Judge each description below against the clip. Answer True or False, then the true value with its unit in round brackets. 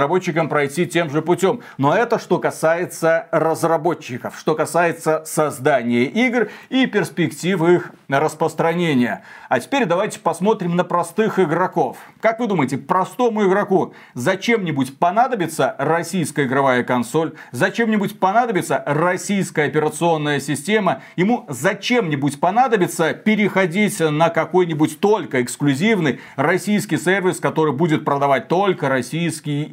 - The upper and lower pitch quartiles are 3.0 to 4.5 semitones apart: True (3.9 semitones)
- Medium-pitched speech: True (170 Hz)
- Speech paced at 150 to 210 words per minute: False (110 wpm)